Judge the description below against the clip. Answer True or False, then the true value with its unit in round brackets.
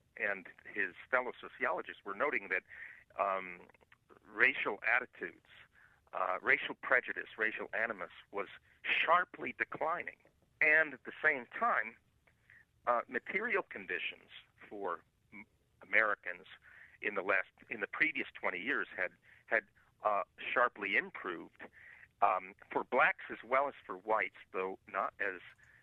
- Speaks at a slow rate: True (125 wpm)